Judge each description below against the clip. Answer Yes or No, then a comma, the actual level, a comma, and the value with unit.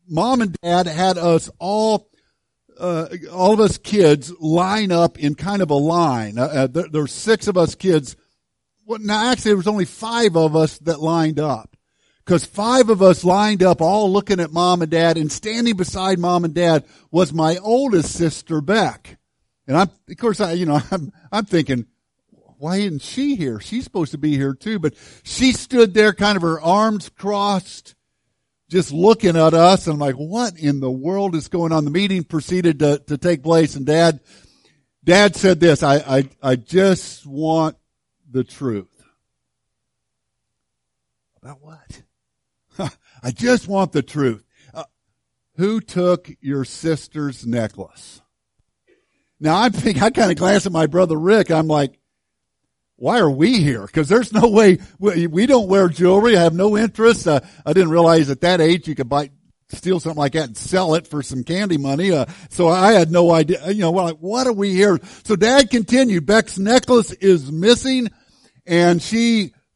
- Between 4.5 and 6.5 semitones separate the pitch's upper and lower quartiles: Yes, average, 4.8 semitones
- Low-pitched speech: No, medium, 175 Hz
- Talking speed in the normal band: Yes, average, 180 wpm